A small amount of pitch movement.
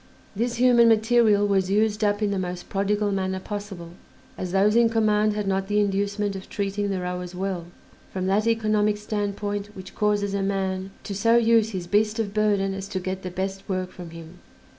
Yes: narrow, 1.8 semitones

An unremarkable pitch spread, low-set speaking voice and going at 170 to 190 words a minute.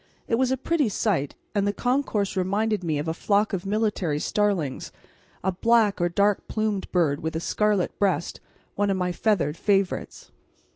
No: average, 3.5 semitones; high, 200 Hz; average, 175 wpm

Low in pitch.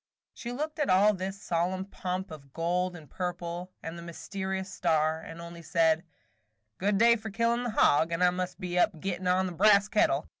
No: medium, 180 Hz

